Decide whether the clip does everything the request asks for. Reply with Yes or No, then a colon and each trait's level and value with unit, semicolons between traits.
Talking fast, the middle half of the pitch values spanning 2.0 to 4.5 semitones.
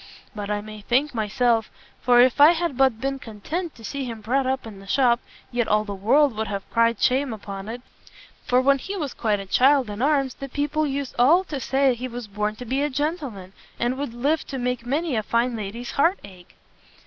Yes: fast, 220 wpm; average, 4.2 semitones